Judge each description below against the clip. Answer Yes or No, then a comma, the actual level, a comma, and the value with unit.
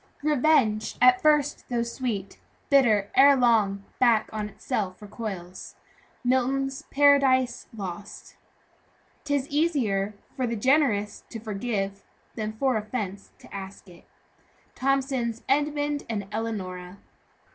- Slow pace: Yes, slow, 110 wpm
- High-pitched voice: Yes, high, 235 Hz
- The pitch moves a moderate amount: Yes, average, 4.9 semitones